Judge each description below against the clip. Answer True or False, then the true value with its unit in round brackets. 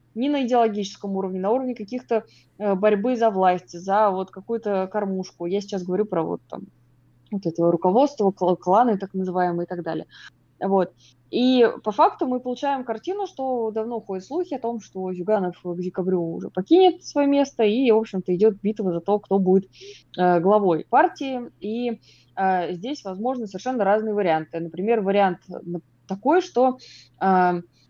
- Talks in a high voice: True (200 Hz)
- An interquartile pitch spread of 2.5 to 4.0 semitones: False (4.8 semitones)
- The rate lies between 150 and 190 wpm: True (160 wpm)